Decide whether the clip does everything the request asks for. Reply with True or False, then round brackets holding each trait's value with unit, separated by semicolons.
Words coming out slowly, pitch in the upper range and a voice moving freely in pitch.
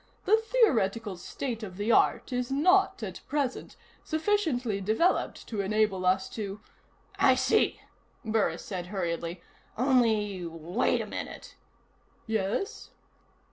True (120 wpm; 220 Hz; 6.1 semitones)